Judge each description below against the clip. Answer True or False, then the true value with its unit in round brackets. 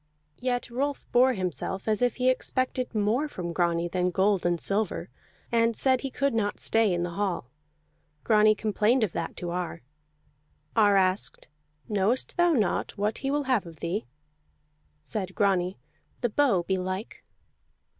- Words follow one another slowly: False (155 wpm)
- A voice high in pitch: True (210 Hz)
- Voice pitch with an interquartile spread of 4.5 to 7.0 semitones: True (5.1 semitones)